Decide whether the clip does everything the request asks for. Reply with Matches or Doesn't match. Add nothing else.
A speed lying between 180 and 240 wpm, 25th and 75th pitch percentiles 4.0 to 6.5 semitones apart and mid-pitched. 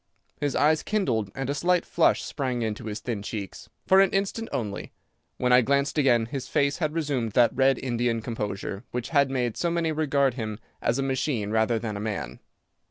Doesn't match